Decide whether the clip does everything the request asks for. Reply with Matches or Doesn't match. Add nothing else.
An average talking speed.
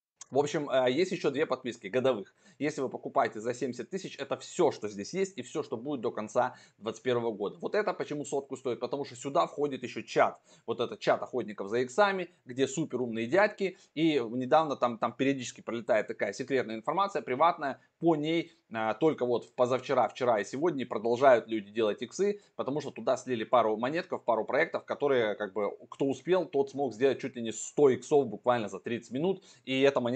Doesn't match